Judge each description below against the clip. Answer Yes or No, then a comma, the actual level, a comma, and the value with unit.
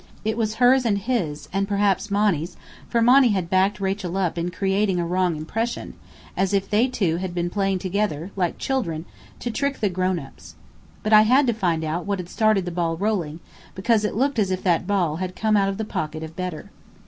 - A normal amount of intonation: Yes, average, 3.5 semitones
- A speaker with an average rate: No, fast, 215 wpm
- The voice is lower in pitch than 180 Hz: No, high, 195 Hz